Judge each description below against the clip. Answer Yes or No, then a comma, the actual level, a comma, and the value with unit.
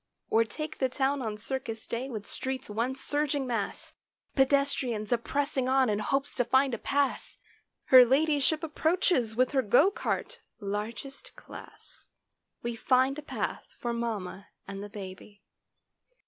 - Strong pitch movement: No, average, 3.9 semitones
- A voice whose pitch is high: Yes, very high, 255 Hz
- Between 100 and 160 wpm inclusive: Yes, average, 145 wpm